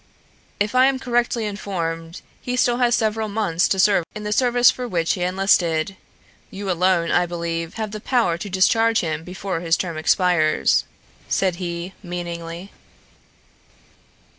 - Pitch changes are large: No, average, 4.2 semitones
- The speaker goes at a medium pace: Yes, average, 150 wpm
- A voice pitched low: No, high, 190 Hz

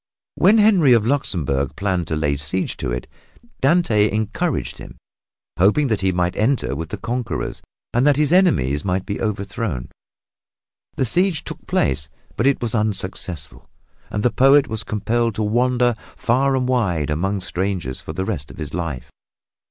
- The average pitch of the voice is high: No, low, 105 Hz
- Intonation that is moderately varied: No, wide, 6.7 semitones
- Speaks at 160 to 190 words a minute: Yes, average, 165 wpm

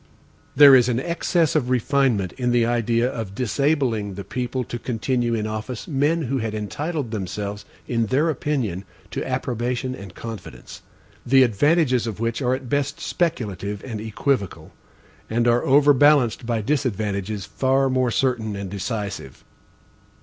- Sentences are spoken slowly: No, average, 145 wpm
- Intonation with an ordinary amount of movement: Yes, average, 3.9 semitones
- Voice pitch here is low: Yes, low, 120 Hz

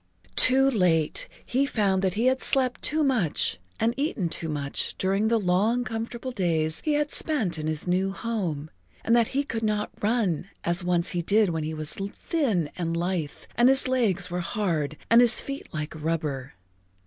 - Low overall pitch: No, high, 195 Hz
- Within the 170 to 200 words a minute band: Yes, average, 185 wpm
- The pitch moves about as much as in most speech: No, wide, 6.3 semitones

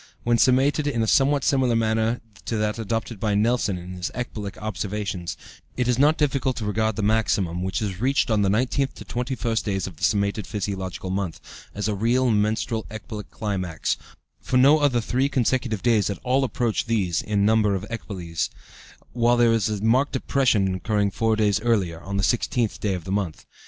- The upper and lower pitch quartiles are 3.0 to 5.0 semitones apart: Yes, average, 3.4 semitones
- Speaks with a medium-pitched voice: No, low, 110 Hz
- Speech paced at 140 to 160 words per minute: No, average, 190 wpm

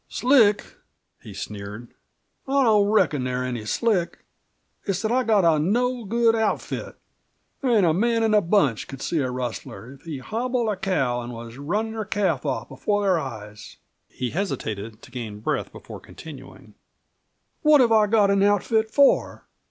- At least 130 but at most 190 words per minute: Yes, average, 170 wpm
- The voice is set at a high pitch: Yes, high, 195 Hz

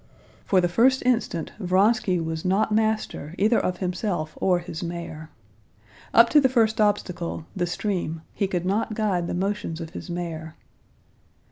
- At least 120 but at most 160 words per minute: Yes, average, 155 wpm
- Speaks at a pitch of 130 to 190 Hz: Yes, medium, 185 Hz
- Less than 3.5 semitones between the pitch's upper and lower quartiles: No, average, 3.9 semitones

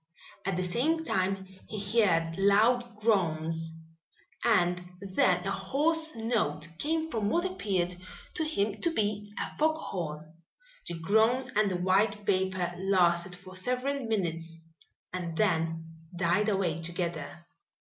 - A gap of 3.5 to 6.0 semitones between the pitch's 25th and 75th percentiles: Yes, average, 4.5 semitones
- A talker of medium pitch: No, high, 195 Hz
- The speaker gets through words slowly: Yes, slow, 130 wpm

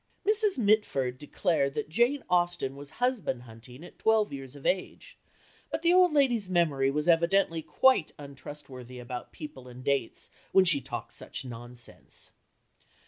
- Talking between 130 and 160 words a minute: Yes, average, 145 wpm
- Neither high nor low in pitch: Yes, medium, 150 Hz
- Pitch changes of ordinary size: No, wide, 7.9 semitones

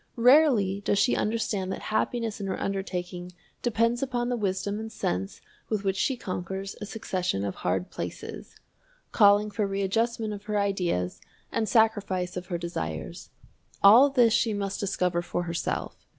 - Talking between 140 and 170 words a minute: Yes, average, 155 wpm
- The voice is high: Yes, high, 200 Hz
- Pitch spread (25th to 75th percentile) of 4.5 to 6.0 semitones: No, average, 3.5 semitones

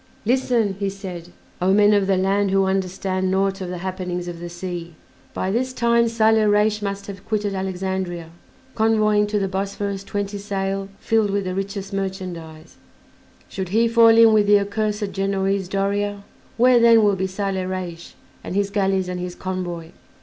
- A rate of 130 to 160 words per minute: No, average, 170 wpm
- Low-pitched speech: No, high, 195 Hz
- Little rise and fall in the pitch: Yes, narrow, 1.8 semitones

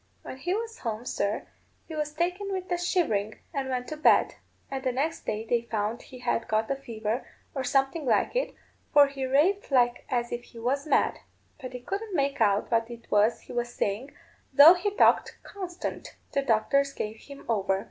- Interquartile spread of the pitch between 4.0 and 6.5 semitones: Yes, average, 5.0 semitones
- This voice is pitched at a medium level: No, very high, 265 Hz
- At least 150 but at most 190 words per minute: No, average, 200 wpm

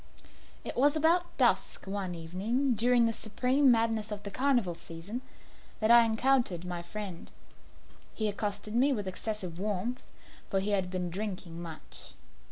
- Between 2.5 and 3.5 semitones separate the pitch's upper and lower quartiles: No, average, 4.7 semitones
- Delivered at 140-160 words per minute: Yes, average, 150 wpm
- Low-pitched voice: No, high, 210 Hz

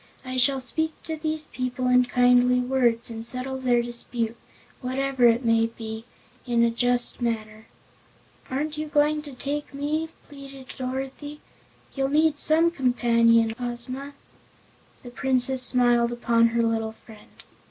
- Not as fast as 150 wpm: Yes, average, 140 wpm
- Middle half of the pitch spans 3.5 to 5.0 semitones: No, average, 2.7 semitones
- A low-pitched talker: No, very high, 250 Hz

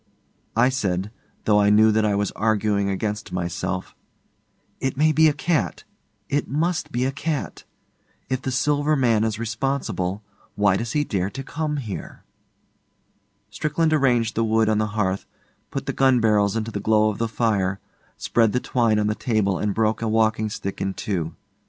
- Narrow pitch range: No, average, 4.1 semitones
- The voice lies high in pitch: No, low, 110 Hz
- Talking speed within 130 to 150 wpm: No, average, 175 wpm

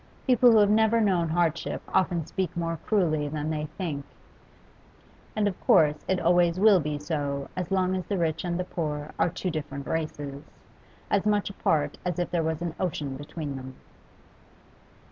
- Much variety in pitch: No, average, 3.8 semitones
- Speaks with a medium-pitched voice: Yes, medium, 170 Hz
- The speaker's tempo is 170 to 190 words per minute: Yes, average, 175 wpm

